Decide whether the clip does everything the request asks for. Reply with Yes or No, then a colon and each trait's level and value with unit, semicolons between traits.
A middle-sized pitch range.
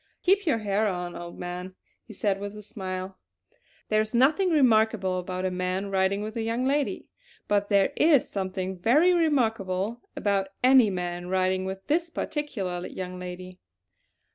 Yes: average, 4.2 semitones